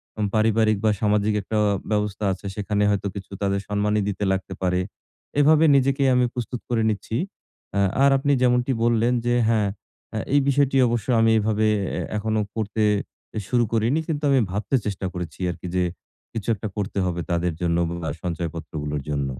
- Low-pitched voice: Yes, low, 105 Hz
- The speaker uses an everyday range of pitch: Yes, average, 3.7 semitones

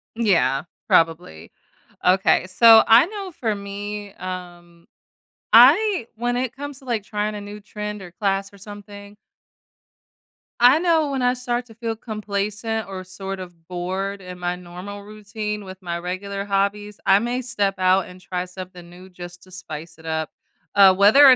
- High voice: Yes, high, 200 Hz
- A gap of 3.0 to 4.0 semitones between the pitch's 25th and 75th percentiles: Yes, average, 3.4 semitones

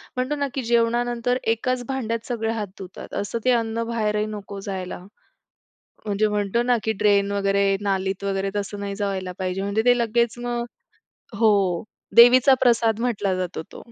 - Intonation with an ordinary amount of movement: Yes, average, 3.1 semitones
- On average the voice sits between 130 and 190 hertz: No, high, 215 Hz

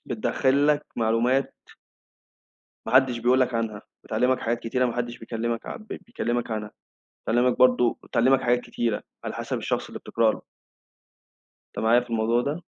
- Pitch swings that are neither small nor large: No, narrow, 1.9 semitones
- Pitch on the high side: No, low, 120 Hz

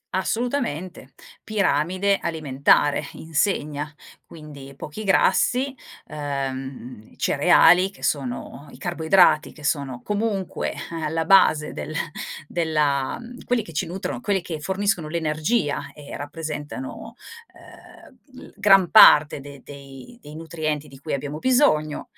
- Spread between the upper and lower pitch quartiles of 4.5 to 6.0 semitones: Yes, average, 4.9 semitones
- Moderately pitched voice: Yes, medium, 155 Hz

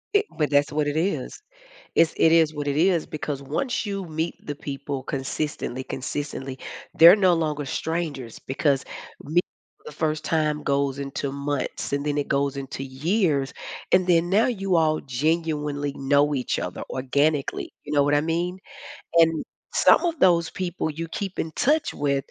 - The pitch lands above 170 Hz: No, medium, 150 Hz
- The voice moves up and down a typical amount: Yes, average, 3.0 semitones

